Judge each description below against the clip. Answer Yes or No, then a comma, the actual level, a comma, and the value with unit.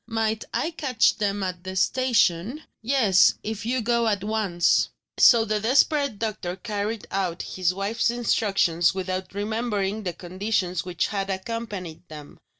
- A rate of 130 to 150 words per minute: Yes, average, 145 wpm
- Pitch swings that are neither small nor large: Yes, average, 3.5 semitones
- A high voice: Yes, high, 205 Hz